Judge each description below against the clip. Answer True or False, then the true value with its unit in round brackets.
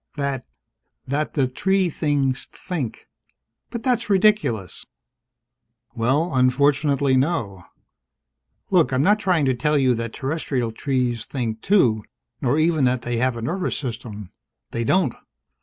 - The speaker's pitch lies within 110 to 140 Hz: True (135 Hz)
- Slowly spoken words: True (130 wpm)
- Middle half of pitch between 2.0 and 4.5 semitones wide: False (5.1 semitones)